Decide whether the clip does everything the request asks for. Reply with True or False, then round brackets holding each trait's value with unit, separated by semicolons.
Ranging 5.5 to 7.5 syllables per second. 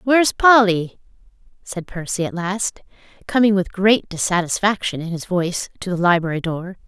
False (5.1 syllables/s)